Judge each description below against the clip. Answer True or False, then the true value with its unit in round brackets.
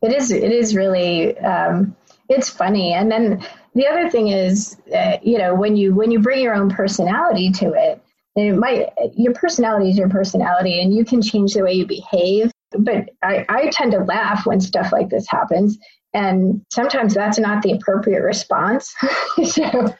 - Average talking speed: True (185 wpm)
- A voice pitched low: False (210 Hz)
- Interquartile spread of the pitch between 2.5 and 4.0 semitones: True (3.0 semitones)